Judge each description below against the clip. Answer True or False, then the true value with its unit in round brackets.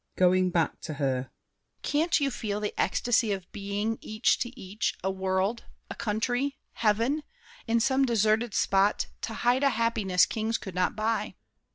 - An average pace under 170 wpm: True (160 wpm)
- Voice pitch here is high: True (215 Hz)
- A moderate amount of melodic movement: True (3.9 semitones)